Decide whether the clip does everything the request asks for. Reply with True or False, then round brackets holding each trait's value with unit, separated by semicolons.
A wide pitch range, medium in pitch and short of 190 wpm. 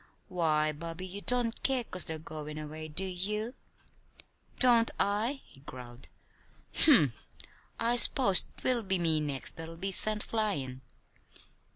True (6.2 semitones; 180 Hz; 135 wpm)